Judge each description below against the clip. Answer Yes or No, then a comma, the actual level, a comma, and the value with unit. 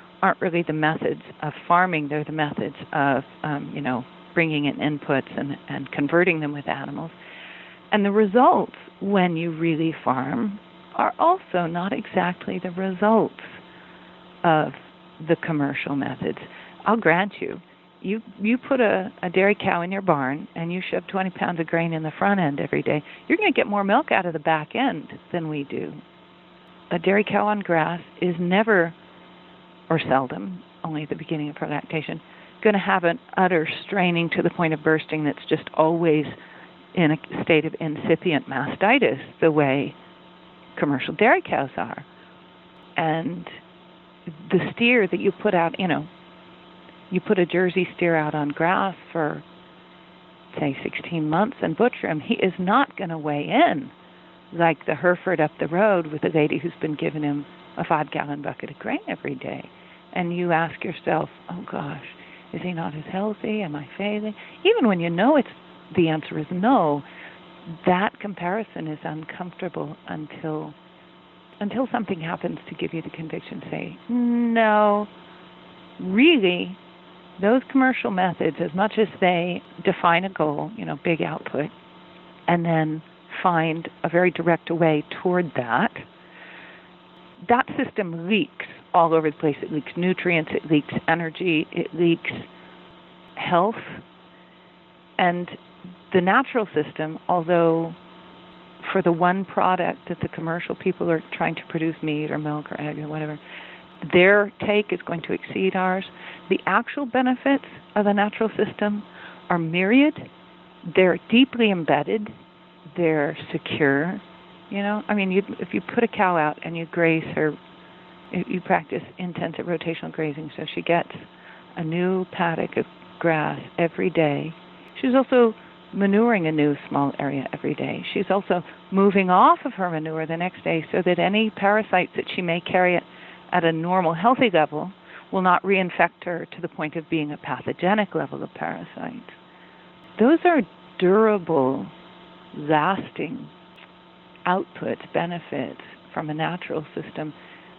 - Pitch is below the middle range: No, medium, 175 Hz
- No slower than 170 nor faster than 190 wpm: No, average, 155 wpm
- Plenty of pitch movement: No, average, 3.5 semitones